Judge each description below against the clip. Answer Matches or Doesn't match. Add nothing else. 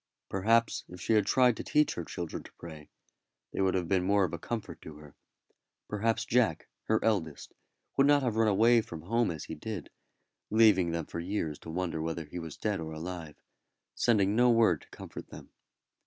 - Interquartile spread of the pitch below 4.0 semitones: Doesn't match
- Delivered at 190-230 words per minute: Matches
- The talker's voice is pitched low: Matches